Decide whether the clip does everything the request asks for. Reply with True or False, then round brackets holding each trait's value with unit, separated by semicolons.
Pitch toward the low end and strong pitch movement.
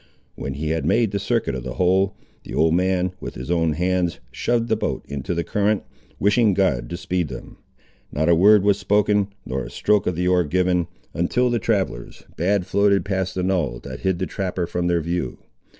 False (90 Hz; 3.0 semitones)